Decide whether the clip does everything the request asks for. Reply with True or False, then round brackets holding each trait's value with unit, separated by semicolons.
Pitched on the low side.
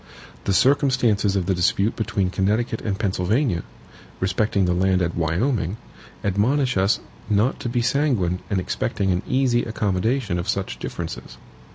True (100 Hz)